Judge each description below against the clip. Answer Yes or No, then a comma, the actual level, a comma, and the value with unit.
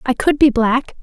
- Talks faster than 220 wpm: Yes, fast, 235 wpm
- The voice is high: Yes, very high, 255 Hz